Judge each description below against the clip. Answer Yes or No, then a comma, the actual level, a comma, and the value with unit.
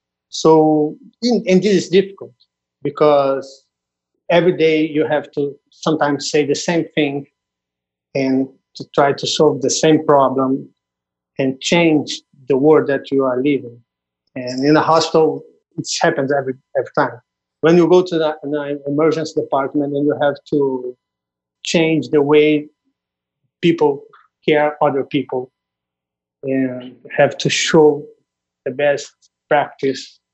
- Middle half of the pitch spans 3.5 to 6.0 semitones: No, average, 3.1 semitones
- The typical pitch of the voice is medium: Yes, medium, 145 Hz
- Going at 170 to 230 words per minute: No, slow, 135 wpm